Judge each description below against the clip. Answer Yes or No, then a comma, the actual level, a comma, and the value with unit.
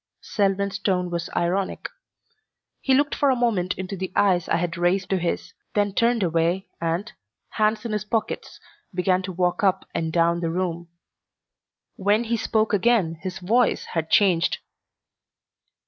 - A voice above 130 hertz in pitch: Yes, high, 190 Hz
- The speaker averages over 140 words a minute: Yes, average, 150 wpm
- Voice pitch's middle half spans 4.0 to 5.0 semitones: No, average, 3.4 semitones